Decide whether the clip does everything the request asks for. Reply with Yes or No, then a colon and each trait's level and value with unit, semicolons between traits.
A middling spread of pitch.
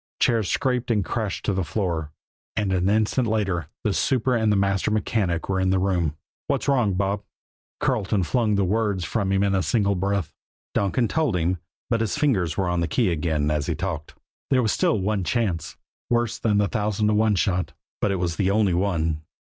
Yes: average, 3.3 semitones